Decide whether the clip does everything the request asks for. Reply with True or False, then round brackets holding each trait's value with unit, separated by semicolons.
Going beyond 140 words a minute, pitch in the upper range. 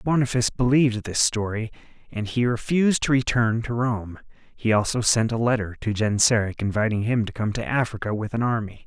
False (185 wpm; 115 Hz)